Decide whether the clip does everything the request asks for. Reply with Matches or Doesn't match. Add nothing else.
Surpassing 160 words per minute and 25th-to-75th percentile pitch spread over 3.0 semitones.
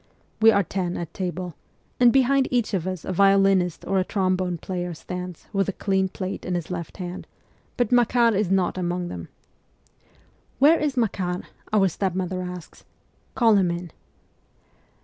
Doesn't match